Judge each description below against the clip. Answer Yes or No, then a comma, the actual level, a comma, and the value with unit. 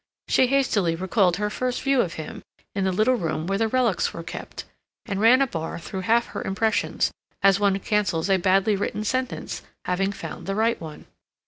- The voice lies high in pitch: Yes, high, 200 Hz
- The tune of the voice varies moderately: Yes, average, 3.8 semitones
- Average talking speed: Yes, average, 195 wpm